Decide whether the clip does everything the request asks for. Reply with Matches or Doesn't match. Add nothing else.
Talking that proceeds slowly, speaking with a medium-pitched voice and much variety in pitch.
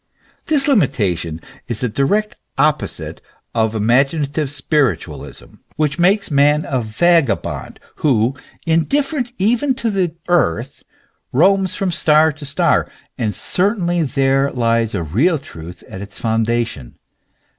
Matches